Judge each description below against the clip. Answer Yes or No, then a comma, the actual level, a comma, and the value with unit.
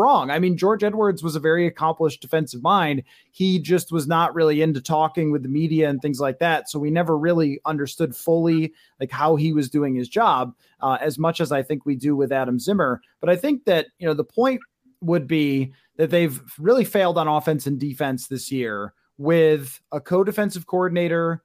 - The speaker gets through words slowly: No, fast, 205 wpm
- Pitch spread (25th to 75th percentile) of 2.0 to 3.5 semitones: Yes, average, 3.1 semitones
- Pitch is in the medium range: Yes, medium, 160 Hz